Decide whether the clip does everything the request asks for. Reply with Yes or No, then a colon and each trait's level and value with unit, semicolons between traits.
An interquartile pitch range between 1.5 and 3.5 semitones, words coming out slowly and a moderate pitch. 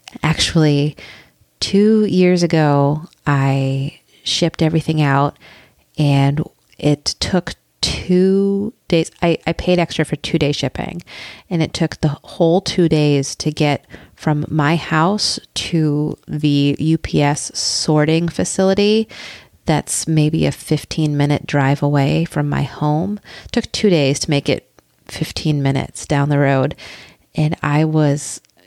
Yes: average, 2.8 semitones; slow, 130 wpm; medium, 155 Hz